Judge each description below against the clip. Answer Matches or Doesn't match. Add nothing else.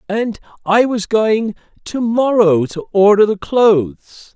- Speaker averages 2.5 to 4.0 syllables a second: Matches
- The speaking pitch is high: Matches